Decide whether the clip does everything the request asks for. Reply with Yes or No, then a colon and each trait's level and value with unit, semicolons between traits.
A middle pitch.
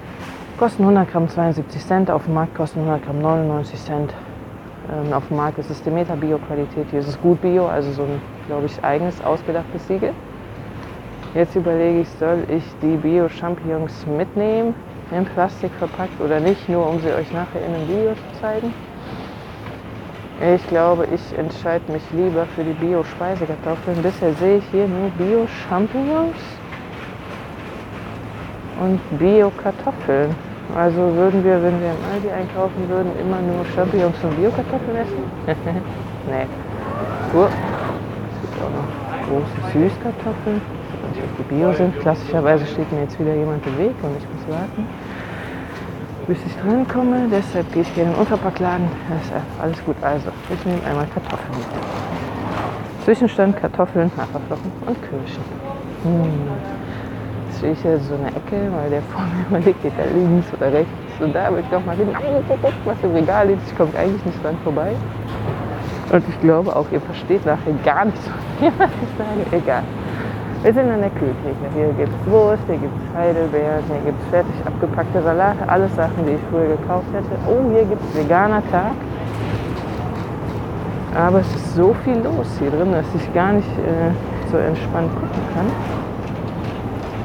Yes: medium, 165 Hz